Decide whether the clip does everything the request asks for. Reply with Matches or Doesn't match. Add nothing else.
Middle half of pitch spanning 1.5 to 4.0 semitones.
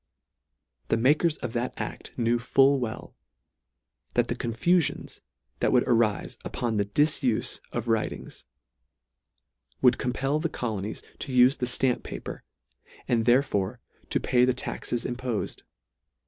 Matches